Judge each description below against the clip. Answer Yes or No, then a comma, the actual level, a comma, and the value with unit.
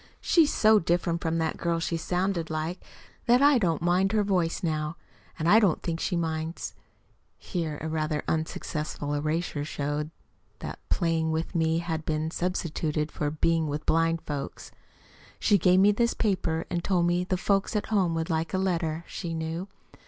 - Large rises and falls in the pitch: No, narrow, 2.5 semitones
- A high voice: No, medium, 165 Hz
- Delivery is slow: No, average, 175 wpm